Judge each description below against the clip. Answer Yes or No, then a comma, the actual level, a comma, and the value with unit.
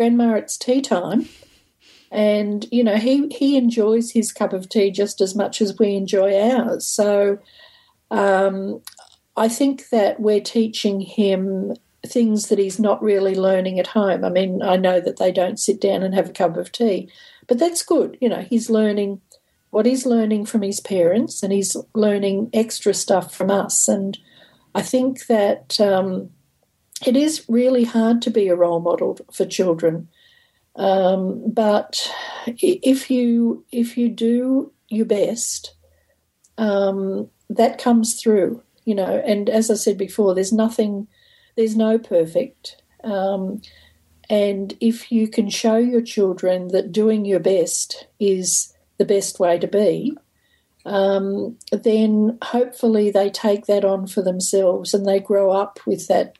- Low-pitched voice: No, high, 210 Hz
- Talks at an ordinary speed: Yes, average, 155 wpm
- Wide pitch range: No, average, 2.9 semitones